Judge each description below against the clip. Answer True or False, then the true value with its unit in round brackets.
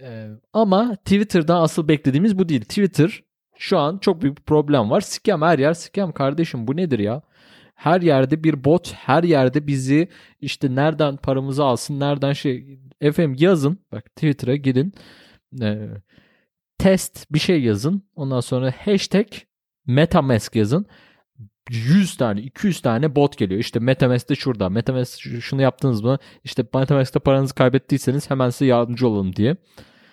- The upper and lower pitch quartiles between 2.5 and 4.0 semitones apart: False (4.4 semitones)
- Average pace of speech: False (145 wpm)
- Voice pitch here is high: False (140 Hz)